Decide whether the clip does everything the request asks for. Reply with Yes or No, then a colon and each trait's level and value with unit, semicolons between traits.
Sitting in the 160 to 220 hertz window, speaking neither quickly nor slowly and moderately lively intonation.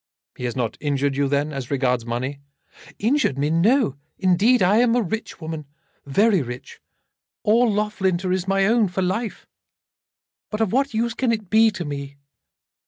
No: medium, 185 Hz; average, 170 wpm; wide, 7.7 semitones